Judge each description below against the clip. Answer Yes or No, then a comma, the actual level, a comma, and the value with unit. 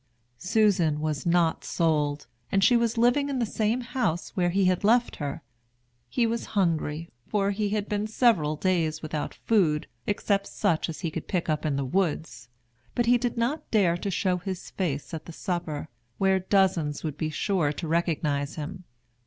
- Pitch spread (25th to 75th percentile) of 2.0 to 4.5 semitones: No, average, 5.1 semitones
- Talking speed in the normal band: Yes, average, 180 wpm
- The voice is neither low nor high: Yes, medium, 180 Hz